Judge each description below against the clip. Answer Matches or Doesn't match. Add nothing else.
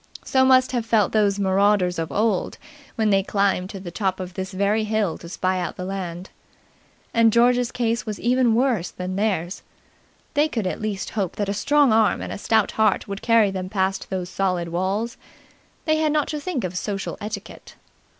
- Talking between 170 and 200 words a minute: Matches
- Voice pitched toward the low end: Doesn't match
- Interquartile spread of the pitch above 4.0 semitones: Doesn't match